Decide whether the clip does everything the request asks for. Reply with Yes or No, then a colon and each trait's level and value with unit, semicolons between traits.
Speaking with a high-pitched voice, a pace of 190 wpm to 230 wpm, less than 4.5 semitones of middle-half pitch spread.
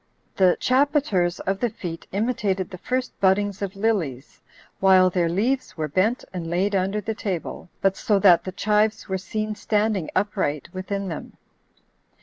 No: high, 195 Hz; average, 155 wpm; narrow, 2.6 semitones